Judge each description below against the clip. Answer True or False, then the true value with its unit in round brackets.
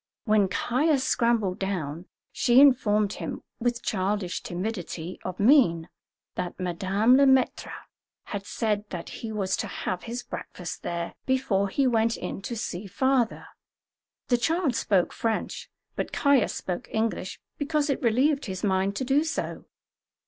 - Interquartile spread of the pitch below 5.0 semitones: False (5.3 semitones)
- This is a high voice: True (215 Hz)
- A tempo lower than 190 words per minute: True (145 wpm)